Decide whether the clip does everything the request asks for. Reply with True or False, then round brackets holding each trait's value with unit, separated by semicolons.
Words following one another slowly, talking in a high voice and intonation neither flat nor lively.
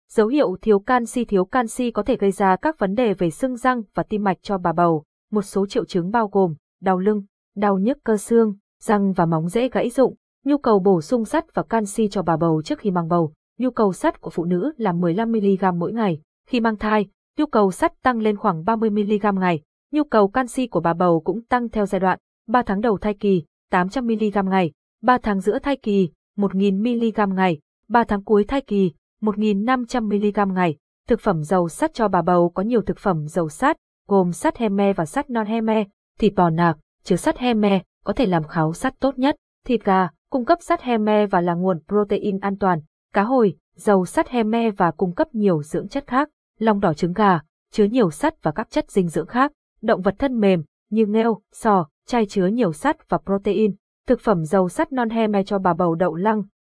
False (220 wpm; 205 Hz; 4.0 semitones)